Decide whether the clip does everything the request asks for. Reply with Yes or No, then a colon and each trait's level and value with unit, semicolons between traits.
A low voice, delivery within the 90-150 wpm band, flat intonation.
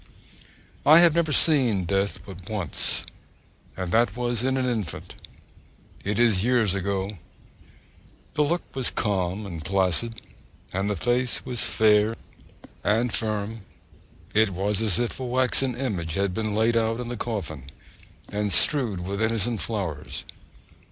No: low, 110 Hz; average, 140 wpm; average, 3.8 semitones